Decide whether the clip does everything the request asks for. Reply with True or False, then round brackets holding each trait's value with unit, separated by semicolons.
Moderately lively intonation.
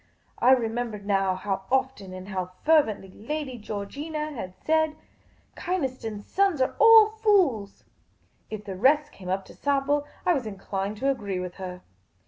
False (7.3 semitones)